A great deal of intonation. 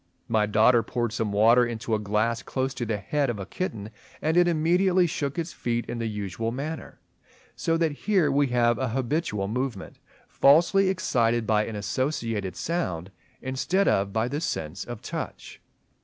Yes: wide, 5.9 semitones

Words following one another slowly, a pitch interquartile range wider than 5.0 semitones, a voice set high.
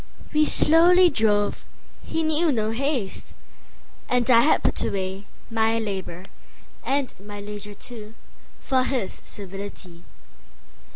Yes: slow, 100 wpm; wide, 5.4 semitones; high, 225 Hz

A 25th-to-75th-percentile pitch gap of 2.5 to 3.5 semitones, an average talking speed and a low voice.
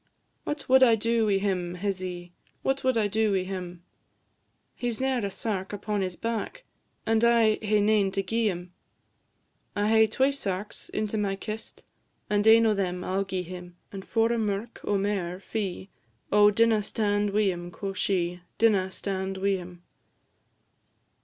No: average, 2.8 semitones; average, 170 wpm; high, 205 Hz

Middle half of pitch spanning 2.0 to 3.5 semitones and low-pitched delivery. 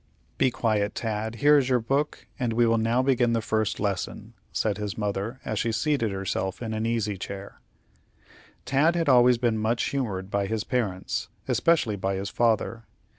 Yes: average, 3.2 semitones; low, 115 Hz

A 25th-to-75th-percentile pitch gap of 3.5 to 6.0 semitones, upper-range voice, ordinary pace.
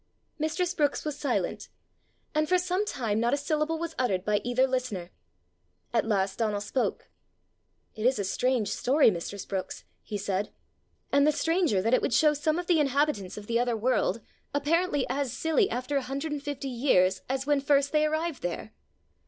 Yes: wide, 5.6 semitones; very high, 270 Hz; average, 185 wpm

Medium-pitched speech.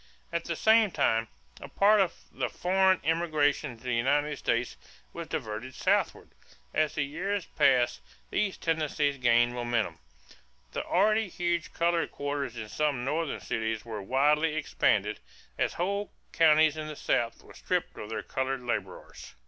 Yes: medium, 145 Hz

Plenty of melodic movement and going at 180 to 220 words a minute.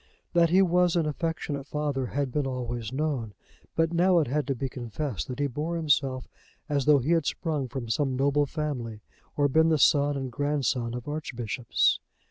No: average, 3.5 semitones; average, 185 wpm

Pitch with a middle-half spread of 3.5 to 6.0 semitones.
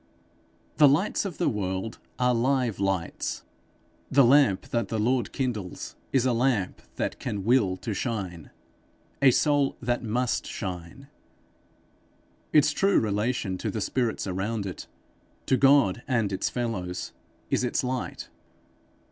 Yes: average, 4.9 semitones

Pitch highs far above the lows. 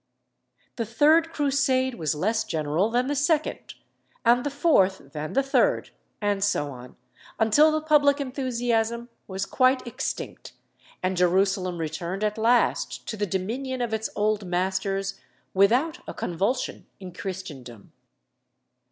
Yes: wide, 5.7 semitones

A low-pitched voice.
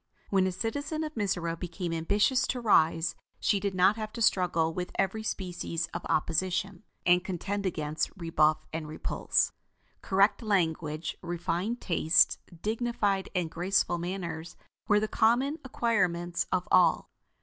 No: medium, 185 Hz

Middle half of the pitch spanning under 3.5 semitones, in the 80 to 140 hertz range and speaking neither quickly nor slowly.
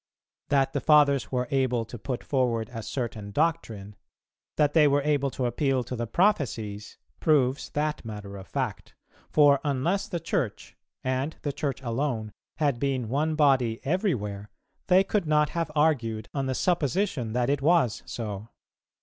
No: average, 4.6 semitones; low, 135 Hz; average, 160 wpm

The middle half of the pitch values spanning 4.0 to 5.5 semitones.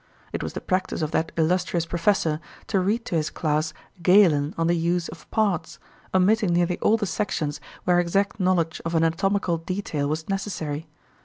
No: average, 3.2 semitones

